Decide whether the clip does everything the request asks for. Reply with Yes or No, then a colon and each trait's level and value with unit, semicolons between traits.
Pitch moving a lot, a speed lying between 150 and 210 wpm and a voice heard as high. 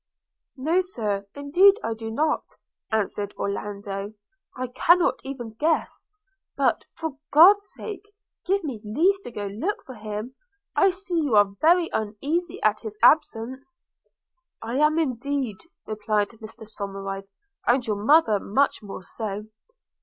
No: wide, 7.3 semitones; average, 140 wpm; high, 240 Hz